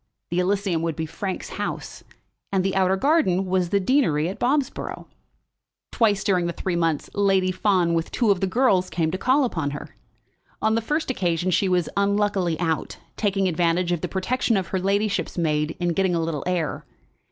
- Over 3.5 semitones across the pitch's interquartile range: No, average, 3.0 semitones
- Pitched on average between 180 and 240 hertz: Yes, medium, 185 Hz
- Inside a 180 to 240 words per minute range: Yes, average, 185 wpm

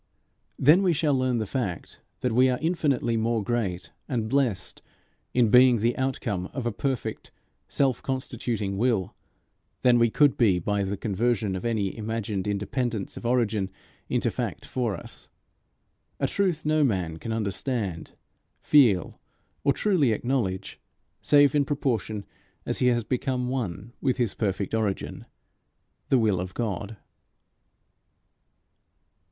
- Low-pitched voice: Yes, low, 115 Hz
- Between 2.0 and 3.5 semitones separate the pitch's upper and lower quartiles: No, average, 4.4 semitones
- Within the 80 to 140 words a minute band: Yes, slow, 135 wpm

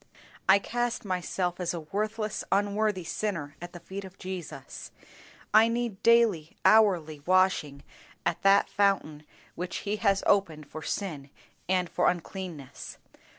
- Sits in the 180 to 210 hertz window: Yes, high, 190 Hz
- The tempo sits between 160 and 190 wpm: No, slow, 135 wpm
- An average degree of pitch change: Yes, average, 3.5 semitones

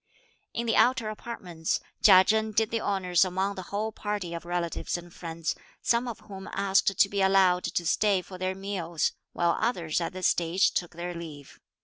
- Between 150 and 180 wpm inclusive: No, average, 190 wpm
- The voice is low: No, high, 190 Hz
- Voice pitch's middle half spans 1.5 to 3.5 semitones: Yes, average, 3.1 semitones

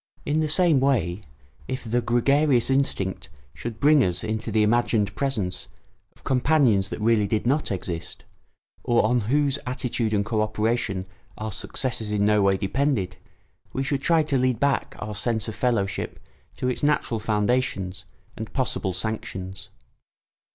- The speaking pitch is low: Yes, low, 115 Hz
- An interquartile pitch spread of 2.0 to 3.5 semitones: No, average, 4.3 semitones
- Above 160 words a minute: No, average, 150 wpm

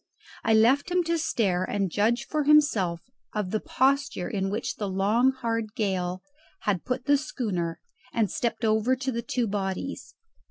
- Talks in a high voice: Yes, high, 220 Hz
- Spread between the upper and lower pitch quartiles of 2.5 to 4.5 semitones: No, average, 5.1 semitones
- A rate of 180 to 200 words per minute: No, average, 165 wpm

